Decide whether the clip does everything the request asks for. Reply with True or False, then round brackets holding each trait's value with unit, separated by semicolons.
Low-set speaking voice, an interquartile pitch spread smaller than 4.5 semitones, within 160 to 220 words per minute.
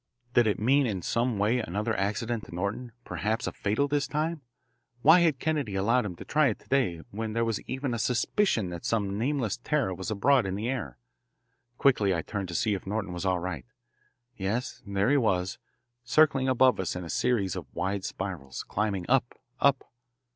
False (110 Hz; 5.1 semitones; 190 wpm)